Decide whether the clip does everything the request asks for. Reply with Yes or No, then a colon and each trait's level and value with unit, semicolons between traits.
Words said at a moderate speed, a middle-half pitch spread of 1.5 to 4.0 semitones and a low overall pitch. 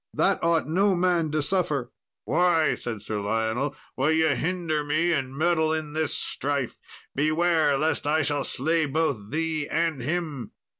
No: average, 155 wpm; average, 2.9 semitones; medium, 155 Hz